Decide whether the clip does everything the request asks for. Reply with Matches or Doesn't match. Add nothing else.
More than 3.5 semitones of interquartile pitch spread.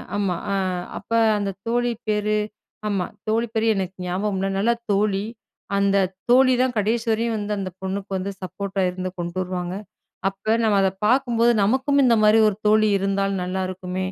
Doesn't match